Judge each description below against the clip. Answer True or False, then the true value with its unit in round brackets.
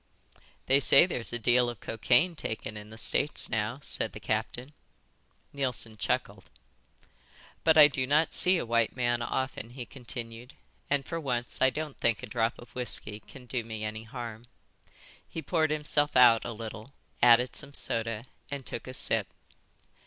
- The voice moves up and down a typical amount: True (3.5 semitones)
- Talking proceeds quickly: False (165 wpm)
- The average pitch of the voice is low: True (120 Hz)